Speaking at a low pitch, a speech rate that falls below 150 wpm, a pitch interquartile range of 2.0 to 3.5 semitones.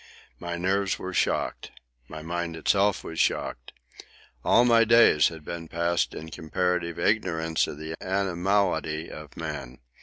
Yes: very low, 85 Hz; average, 140 wpm; average, 3.2 semitones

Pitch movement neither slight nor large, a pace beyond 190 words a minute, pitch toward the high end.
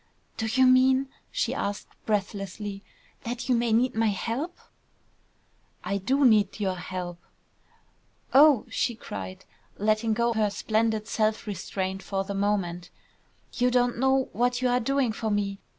No: average, 3.7 semitones; average, 145 wpm; high, 220 Hz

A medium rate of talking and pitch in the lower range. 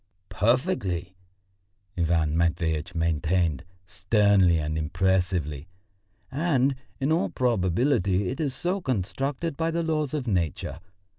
No: slow, 105 wpm; very low, 95 Hz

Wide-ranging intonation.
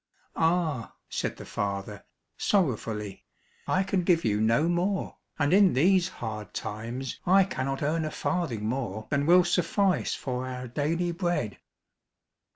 Yes: wide, 7.5 semitones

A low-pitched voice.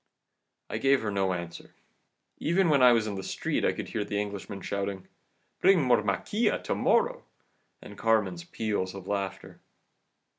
Yes: low, 105 Hz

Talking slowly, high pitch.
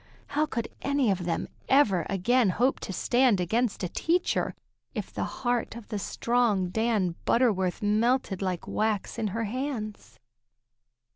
No: average, 145 wpm; high, 220 Hz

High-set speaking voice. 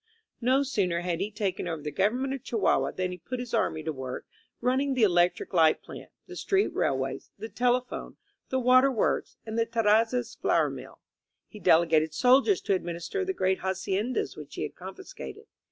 Yes: high, 215 Hz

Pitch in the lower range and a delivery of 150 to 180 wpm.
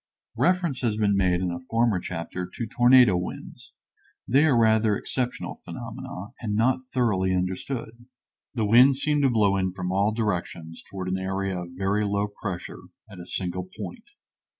Yes: low, 105 Hz; average, 165 wpm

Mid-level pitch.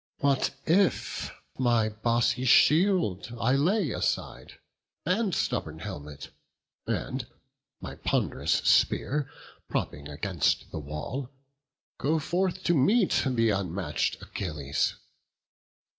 No: low, 120 Hz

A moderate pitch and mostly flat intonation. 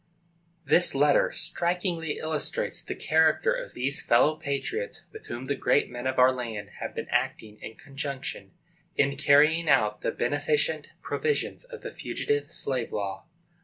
No: medium, 145 Hz; average, 4.3 semitones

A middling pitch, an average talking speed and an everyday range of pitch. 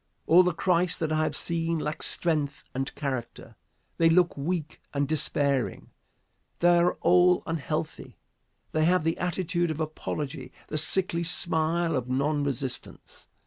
Yes: medium, 160 Hz; average, 145 wpm; average, 3.1 semitones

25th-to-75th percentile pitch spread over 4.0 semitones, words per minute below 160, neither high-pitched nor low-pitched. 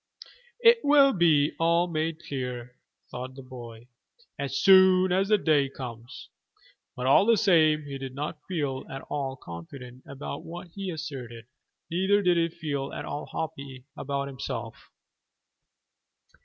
Yes: average, 4.9 semitones; average, 140 wpm; medium, 145 Hz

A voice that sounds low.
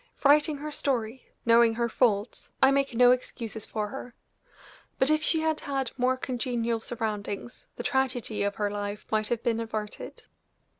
No: high, 240 Hz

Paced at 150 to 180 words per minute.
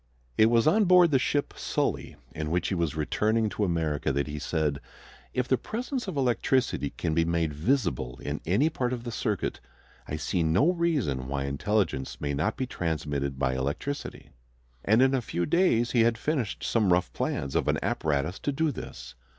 No: average, 190 wpm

